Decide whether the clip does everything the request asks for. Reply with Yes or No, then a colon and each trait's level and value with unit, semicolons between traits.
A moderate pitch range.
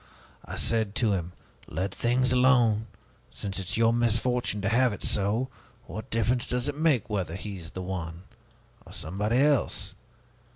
Yes: average, 4.2 semitones